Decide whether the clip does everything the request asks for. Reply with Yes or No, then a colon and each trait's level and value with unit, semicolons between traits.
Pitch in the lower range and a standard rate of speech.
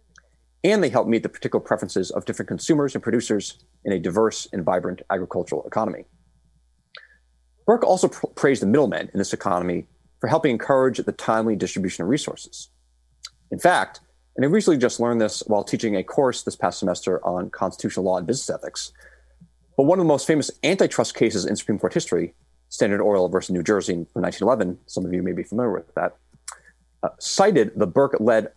Yes: very low, 90 Hz; average, 185 wpm